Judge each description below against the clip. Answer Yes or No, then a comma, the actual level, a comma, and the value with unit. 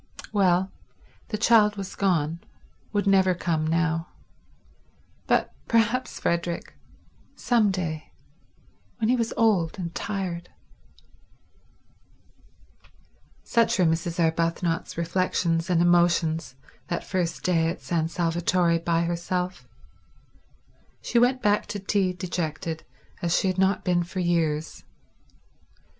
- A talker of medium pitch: Yes, medium, 175 Hz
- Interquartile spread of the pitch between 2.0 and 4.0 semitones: Yes, average, 2.7 semitones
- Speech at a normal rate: No, slow, 105 wpm